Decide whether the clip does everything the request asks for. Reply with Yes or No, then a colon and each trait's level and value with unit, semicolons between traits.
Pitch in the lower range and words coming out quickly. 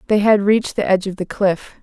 No: high, 200 Hz; fast, 265 wpm